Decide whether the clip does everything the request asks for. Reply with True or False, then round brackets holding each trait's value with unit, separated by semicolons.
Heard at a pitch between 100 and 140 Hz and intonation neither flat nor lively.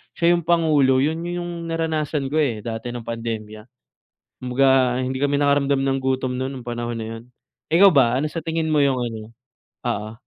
True (135 Hz; 4.6 semitones)